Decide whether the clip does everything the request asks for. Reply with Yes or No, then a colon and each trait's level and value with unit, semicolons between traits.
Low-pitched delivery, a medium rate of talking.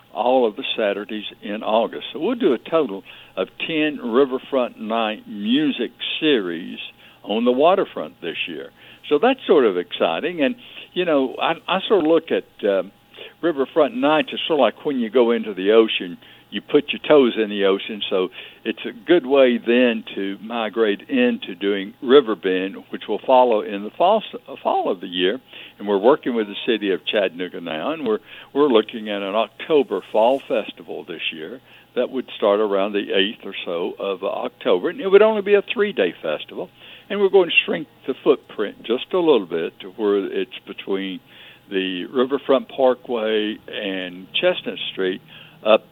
Yes: low, 125 Hz; average, 180 wpm